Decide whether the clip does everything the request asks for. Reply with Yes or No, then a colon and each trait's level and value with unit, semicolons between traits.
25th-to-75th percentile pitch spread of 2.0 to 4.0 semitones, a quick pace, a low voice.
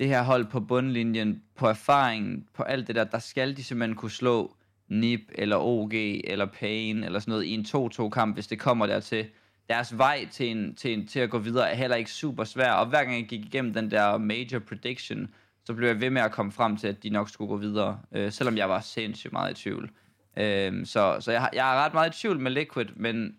Yes: average, 2.9 semitones; fast, 245 wpm; low, 115 Hz